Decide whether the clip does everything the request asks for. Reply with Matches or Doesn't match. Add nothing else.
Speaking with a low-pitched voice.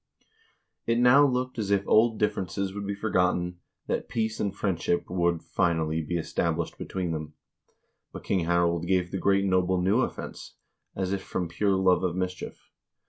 Matches